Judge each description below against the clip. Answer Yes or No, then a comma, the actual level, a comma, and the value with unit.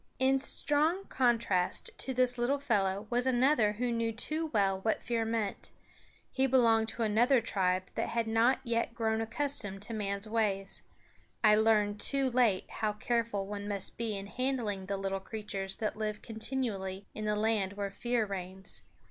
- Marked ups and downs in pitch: No, average, 3.3 semitones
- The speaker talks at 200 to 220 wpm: No, average, 165 wpm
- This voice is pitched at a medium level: No, high, 220 Hz